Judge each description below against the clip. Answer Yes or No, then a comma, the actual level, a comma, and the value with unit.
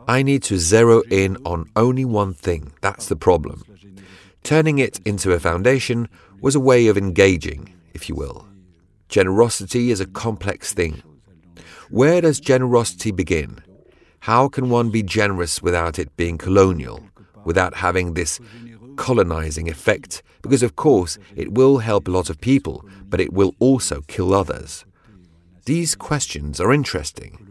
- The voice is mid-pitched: No, low, 100 Hz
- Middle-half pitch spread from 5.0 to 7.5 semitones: Yes, average, 5.3 semitones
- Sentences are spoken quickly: No, average, 150 wpm